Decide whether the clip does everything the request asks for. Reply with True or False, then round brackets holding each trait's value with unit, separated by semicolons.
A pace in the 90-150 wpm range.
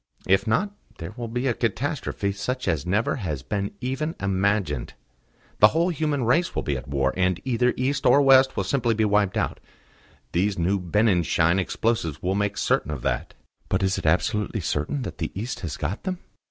False (190 wpm)